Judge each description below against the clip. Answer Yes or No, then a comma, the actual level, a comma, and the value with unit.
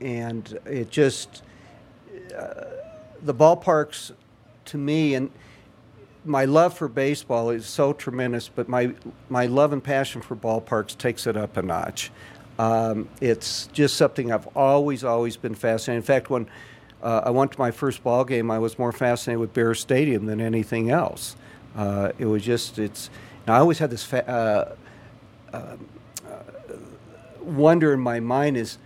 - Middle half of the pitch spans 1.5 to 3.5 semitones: Yes, average, 3.1 semitones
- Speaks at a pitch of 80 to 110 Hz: No, low, 120 Hz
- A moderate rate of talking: Yes, average, 160 wpm